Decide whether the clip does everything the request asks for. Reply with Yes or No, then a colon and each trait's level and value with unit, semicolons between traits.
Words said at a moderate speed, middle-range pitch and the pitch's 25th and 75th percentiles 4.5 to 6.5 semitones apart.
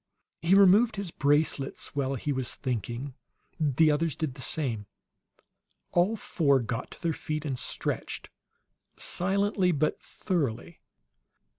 No: slow, 125 wpm; medium, 150 Hz; average, 4.9 semitones